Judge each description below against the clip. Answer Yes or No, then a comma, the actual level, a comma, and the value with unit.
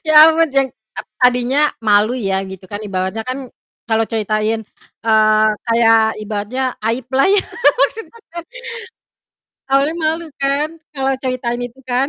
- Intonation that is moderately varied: Yes, average, 4.1 semitones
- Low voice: No, high, 245 Hz